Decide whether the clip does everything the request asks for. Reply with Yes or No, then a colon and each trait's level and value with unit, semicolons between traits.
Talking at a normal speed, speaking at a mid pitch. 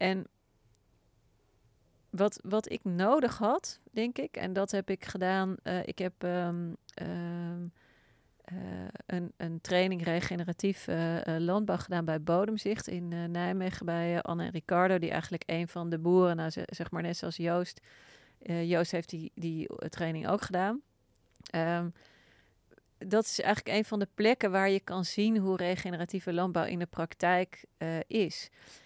Yes: average, 160 wpm; medium, 175 Hz